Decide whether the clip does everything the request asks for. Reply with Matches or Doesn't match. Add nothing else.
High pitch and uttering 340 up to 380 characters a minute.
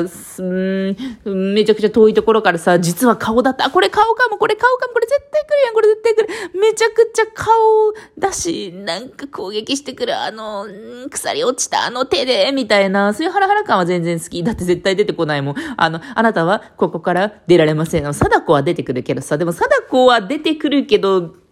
Doesn't match